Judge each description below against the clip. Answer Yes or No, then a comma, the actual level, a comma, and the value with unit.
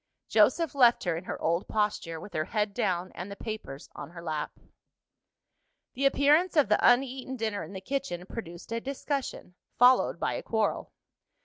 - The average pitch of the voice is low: No, high, 215 Hz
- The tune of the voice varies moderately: No, wide, 6.7 semitones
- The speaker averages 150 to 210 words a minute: Yes, average, 175 wpm